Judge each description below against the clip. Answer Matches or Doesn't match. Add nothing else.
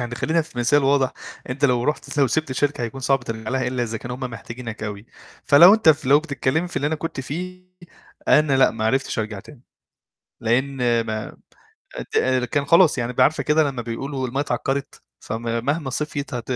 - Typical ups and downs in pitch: Matches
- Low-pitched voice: Matches